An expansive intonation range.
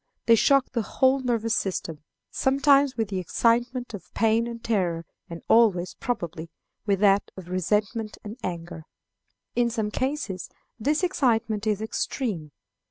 No: average, 4.4 semitones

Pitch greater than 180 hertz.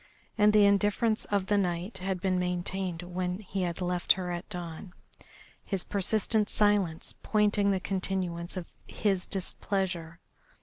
Yes: high, 190 Hz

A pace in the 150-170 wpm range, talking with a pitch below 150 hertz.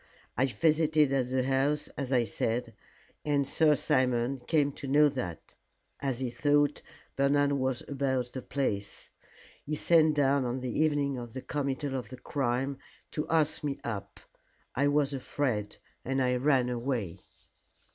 Yes: average, 155 wpm; low, 135 Hz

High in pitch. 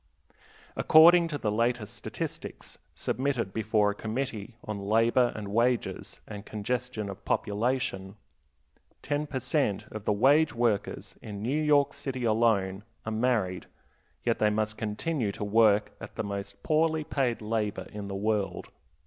No: low, 110 Hz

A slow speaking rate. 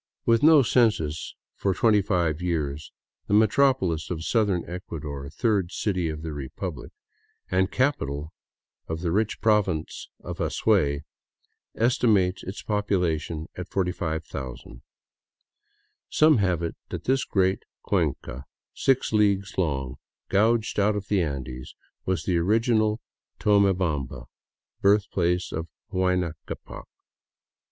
Yes: slow, 120 wpm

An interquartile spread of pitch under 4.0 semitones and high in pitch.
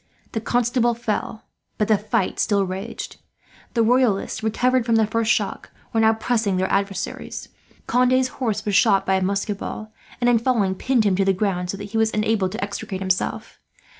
Yes: average, 2.9 semitones; high, 215 Hz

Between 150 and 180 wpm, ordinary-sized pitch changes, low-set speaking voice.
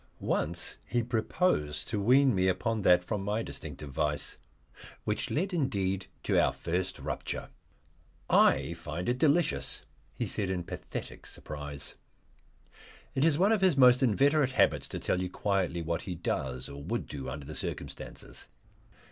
No: average, 155 wpm; wide, 7.7 semitones; very low, 95 Hz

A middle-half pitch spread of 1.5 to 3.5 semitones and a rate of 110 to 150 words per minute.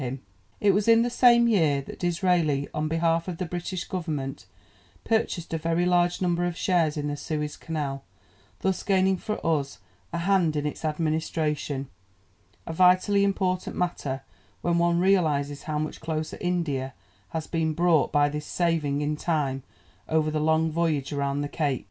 No: average, 3.1 semitones; average, 165 wpm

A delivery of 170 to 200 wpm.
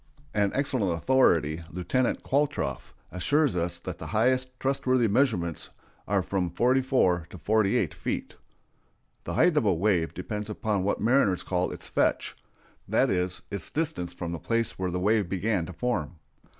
No: average, 160 wpm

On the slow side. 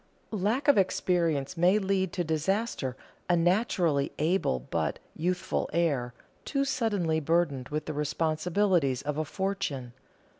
Yes: slow, 125 wpm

